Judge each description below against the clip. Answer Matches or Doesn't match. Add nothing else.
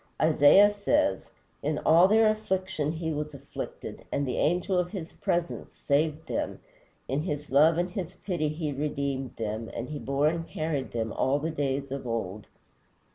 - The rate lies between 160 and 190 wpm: Matches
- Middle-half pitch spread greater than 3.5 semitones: Matches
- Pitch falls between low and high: Matches